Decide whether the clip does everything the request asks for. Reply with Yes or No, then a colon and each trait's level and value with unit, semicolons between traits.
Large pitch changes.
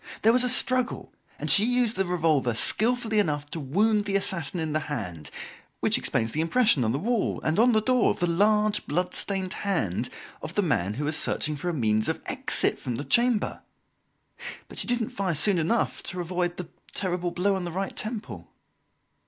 Yes: wide, 6.0 semitones